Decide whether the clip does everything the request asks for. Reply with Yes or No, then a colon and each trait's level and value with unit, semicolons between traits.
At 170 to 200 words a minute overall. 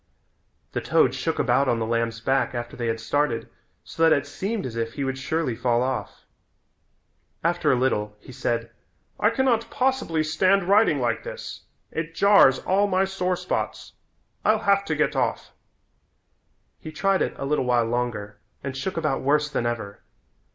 Yes: average, 175 wpm